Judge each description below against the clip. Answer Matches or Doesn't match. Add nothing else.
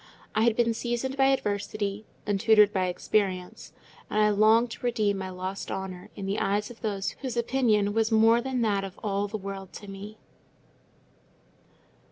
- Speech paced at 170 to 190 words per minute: Matches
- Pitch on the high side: Matches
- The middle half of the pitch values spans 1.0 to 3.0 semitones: Matches